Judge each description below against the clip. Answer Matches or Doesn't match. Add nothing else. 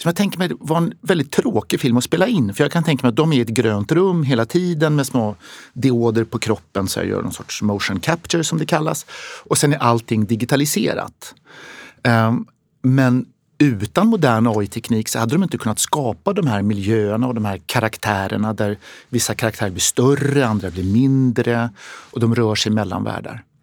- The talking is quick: Matches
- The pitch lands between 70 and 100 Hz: Doesn't match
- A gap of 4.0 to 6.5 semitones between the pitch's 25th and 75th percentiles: Matches